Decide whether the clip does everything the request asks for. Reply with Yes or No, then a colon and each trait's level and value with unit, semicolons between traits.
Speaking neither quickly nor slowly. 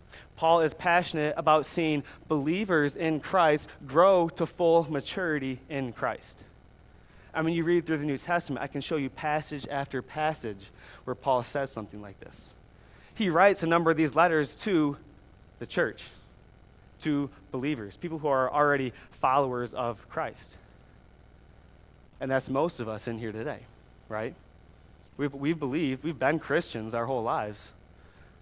Yes: average, 150 wpm